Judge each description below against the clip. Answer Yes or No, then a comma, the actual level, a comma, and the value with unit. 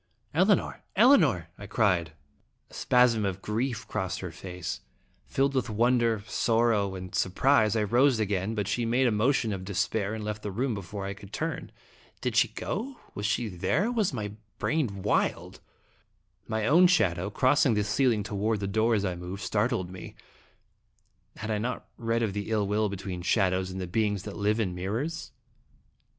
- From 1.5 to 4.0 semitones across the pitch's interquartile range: Yes, average, 3.6 semitones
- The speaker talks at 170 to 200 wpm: Yes, average, 175 wpm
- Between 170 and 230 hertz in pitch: No, low, 105 Hz